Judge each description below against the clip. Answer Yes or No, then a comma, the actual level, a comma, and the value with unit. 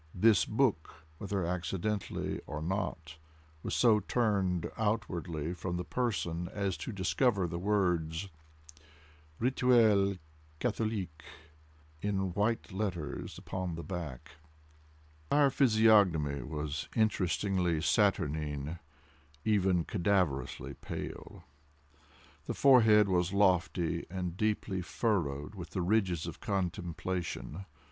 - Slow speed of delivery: Yes, slow, 100 wpm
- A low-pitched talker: Yes, very low, 95 Hz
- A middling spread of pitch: Yes, average, 4.0 semitones